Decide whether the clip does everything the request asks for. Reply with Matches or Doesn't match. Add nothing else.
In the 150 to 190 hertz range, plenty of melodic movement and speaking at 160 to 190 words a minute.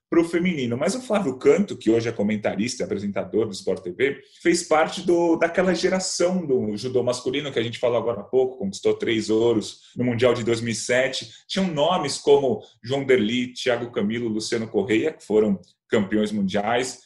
Doesn't match